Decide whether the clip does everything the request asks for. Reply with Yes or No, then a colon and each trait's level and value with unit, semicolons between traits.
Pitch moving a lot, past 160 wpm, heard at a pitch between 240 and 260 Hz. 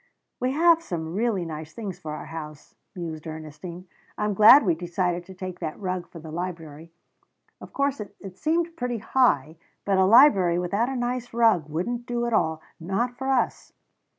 No: wide, 6.6 semitones; average, 180 wpm; medium, 185 Hz